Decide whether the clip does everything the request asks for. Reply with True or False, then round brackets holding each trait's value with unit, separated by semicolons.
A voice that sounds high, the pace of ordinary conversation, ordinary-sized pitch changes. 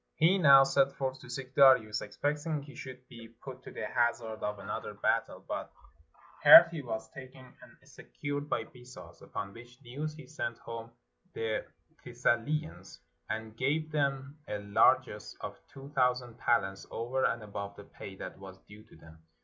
False (125 Hz; 165 wpm; 3.9 semitones)